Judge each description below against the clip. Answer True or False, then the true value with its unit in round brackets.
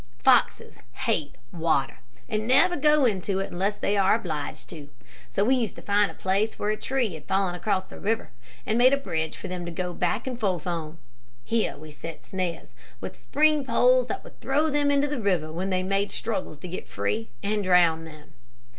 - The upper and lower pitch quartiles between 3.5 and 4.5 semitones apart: False (5.5 semitones)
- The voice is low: False (195 Hz)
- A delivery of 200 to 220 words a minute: True (205 wpm)